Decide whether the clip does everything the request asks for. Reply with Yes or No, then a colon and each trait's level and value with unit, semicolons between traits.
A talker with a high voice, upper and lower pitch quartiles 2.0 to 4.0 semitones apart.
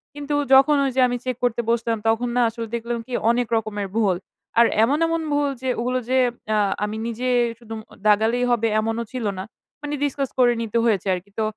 Yes: high, 235 Hz; narrow, 2.6 semitones